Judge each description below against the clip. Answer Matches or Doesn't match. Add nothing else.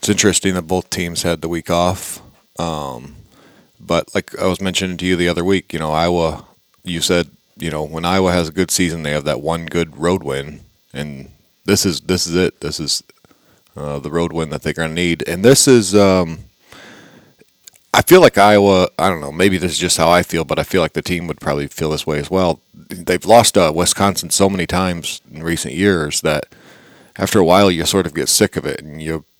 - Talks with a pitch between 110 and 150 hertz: Doesn't match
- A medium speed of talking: Doesn't match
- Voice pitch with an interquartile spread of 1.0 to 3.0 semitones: Matches